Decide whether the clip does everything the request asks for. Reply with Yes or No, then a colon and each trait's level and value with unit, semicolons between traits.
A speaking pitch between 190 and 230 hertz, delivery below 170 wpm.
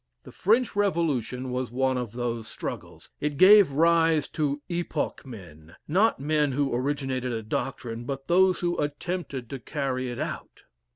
No: medium, 140 Hz; average, 155 wpm